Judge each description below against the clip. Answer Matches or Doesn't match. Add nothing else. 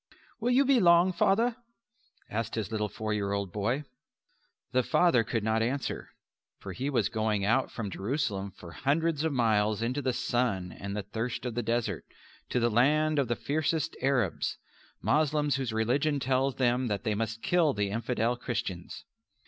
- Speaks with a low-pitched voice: Matches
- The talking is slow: Doesn't match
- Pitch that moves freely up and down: Doesn't match